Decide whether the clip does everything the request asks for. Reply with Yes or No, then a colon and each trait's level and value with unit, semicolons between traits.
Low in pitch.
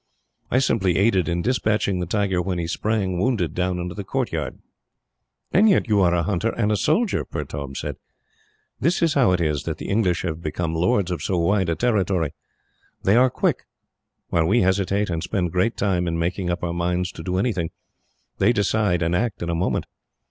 Yes: very low, 95 Hz